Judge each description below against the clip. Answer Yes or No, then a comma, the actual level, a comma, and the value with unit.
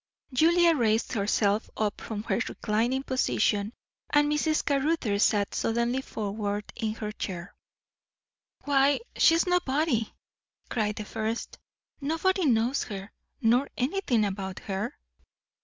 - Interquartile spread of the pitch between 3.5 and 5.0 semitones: No, wide, 5.4 semitones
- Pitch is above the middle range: Yes, high, 230 Hz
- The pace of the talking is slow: Yes, slow, 120 wpm